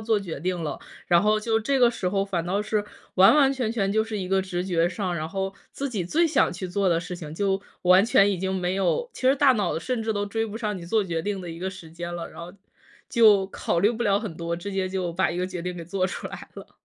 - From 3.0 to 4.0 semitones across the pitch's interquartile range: Yes, average, 3.5 semitones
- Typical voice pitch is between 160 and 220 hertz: Yes, high, 190 Hz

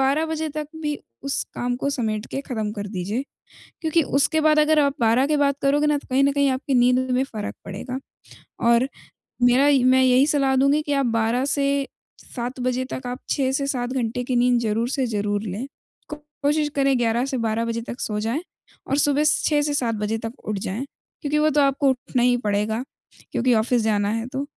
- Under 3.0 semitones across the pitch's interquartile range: No, average, 3.6 semitones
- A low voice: No, very high, 255 Hz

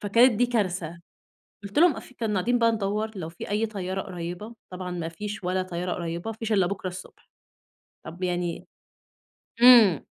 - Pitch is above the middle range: Yes, high, 195 Hz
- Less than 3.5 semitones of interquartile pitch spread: No, average, 3.8 semitones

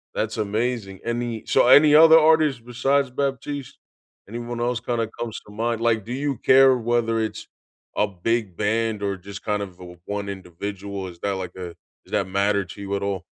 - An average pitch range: Yes, average, 3.4 semitones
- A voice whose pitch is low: Yes, low, 110 Hz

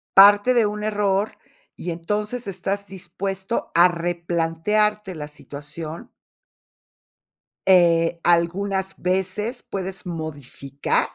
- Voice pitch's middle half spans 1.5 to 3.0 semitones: No, average, 3.5 semitones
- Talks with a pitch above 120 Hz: Yes, high, 190 Hz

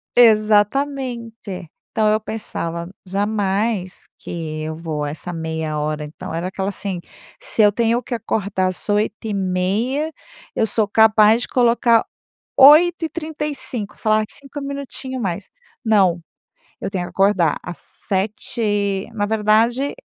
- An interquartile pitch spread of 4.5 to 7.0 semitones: No, average, 4.1 semitones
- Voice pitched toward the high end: Yes, high, 210 Hz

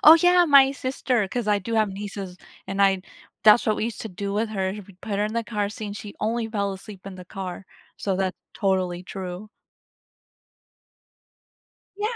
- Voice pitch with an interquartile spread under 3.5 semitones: Yes, average, 2.8 semitones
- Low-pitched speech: No, high, 205 Hz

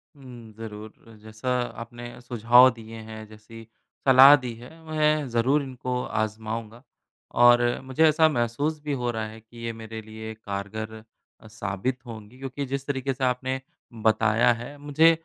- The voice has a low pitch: Yes, low, 120 Hz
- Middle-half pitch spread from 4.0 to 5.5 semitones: No, average, 3.1 semitones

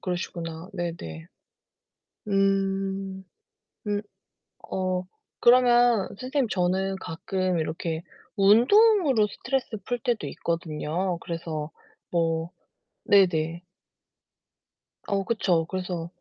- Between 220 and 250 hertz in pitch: No, high, 190 Hz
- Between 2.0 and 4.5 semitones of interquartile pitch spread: Yes, average, 3.7 semitones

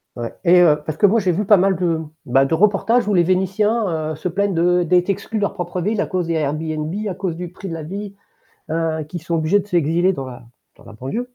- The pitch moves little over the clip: No, average, 3.6 semitones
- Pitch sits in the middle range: Yes, medium, 175 Hz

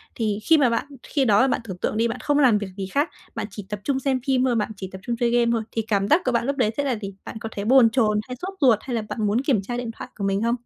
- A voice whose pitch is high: Yes, high, 235 Hz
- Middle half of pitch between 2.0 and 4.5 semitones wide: Yes, average, 3.8 semitones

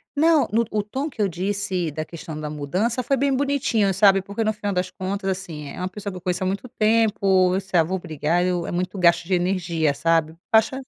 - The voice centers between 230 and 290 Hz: No, high, 190 Hz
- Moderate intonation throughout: Yes, average, 3.5 semitones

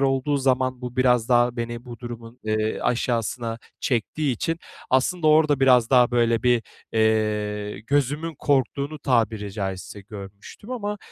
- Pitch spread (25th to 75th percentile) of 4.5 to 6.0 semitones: No, average, 3.4 semitones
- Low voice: Yes, low, 120 Hz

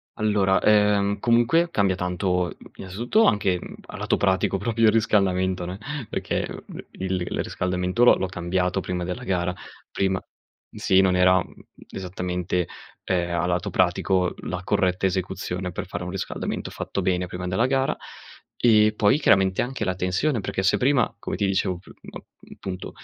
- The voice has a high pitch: No, very low, 95 Hz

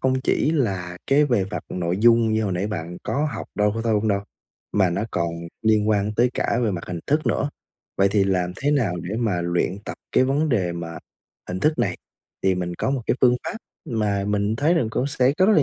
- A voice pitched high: No, low, 105 Hz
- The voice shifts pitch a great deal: Yes, wide, 5.8 semitones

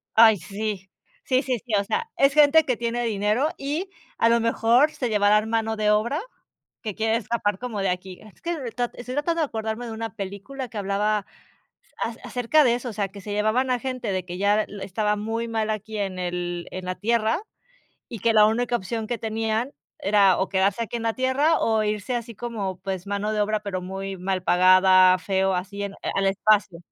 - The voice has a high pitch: Yes, high, 215 Hz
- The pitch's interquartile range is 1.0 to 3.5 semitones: Yes, average, 3.2 semitones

